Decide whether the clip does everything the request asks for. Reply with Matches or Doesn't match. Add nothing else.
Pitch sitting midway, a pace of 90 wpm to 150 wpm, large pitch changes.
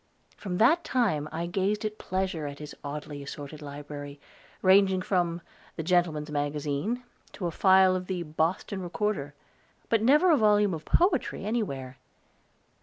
Matches